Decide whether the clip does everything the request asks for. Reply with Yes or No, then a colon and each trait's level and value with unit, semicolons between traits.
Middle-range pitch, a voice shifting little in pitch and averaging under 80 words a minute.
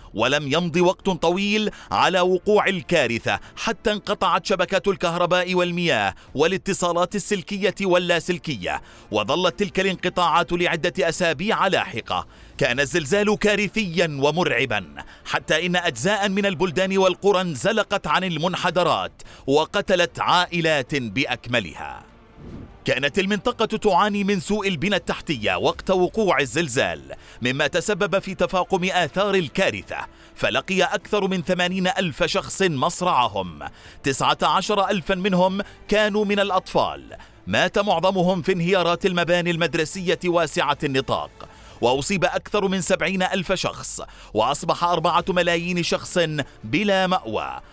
No: medium, 180 Hz; narrow, 2.3 semitones; average, 110 wpm